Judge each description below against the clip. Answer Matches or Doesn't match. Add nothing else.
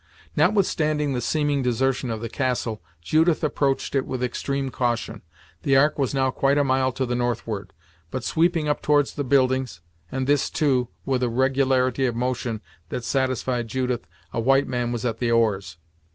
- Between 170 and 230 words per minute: Matches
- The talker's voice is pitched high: Doesn't match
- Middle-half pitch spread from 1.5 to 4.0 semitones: Matches